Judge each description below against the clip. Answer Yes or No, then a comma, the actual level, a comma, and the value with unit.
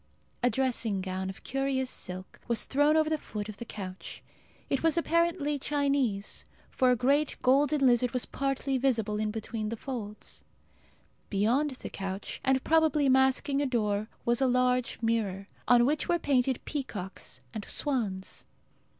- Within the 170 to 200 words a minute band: No, average, 155 wpm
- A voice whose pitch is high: Yes, very high, 250 Hz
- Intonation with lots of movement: No, average, 4.6 semitones